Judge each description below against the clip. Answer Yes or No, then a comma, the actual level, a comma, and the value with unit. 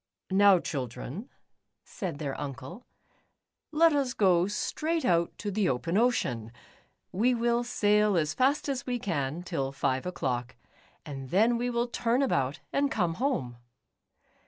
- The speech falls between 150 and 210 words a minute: No, average, 140 wpm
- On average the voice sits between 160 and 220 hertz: Yes, high, 190 Hz